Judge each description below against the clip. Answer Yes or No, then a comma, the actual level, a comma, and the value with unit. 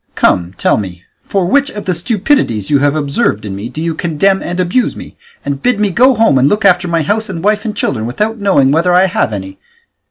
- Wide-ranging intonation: Yes, wide, 7.2 semitones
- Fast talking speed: Yes, fast, 230 wpm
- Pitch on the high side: No, medium, 175 Hz